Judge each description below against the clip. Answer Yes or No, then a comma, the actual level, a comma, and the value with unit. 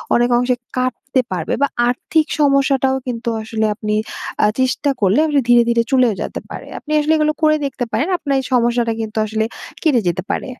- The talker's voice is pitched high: Yes, very high, 250 Hz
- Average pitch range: Yes, average, 3.3 semitones